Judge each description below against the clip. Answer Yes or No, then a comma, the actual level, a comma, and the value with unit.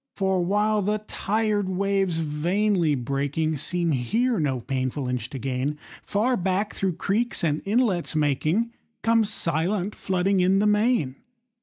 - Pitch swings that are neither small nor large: No, wide, 5.7 semitones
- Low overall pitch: No, medium, 185 Hz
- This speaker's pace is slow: Yes, slow, 125 wpm